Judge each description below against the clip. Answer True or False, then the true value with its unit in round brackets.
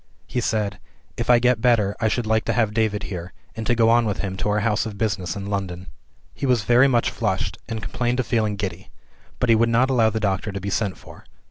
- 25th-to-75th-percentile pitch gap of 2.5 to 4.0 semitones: True (2.8 semitones)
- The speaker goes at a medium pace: False (245 wpm)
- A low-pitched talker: True (110 Hz)